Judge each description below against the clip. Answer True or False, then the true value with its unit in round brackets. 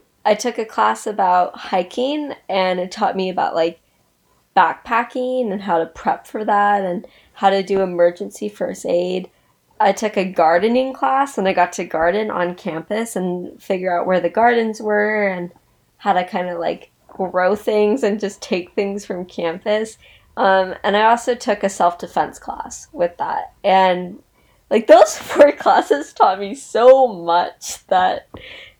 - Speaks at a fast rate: False (165 wpm)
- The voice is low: False (195 Hz)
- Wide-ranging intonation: False (4.0 semitones)